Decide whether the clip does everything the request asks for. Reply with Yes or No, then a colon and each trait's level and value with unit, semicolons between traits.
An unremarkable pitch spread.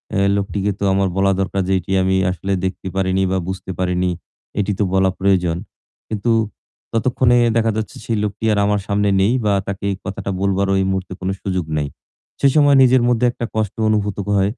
No: narrow, 2.0 semitones